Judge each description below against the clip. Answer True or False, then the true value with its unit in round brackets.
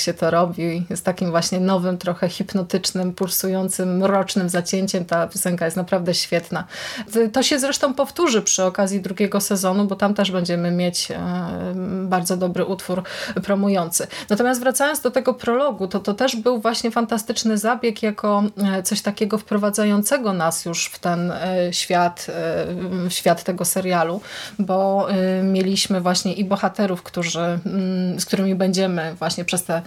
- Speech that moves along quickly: False (140 wpm)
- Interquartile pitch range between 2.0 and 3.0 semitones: True (2.5 semitones)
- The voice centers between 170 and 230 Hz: True (190 Hz)